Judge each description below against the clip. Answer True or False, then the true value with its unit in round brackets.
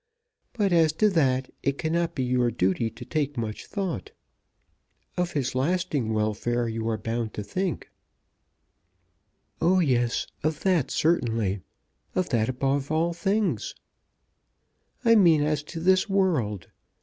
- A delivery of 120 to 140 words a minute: True (135 wpm)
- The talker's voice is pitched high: False (140 Hz)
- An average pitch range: False (6.8 semitones)